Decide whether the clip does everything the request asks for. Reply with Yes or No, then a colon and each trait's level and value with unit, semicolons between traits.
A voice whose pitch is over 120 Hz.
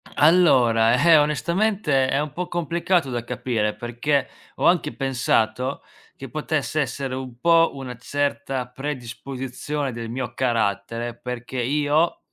Yes: low, 135 Hz